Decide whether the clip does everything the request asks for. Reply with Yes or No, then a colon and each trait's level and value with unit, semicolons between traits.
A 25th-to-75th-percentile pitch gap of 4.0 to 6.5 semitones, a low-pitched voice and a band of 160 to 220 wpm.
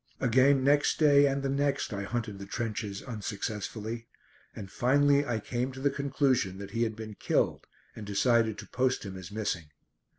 Yes: average, 4.8 semitones; low, 115 Hz; average, 175 wpm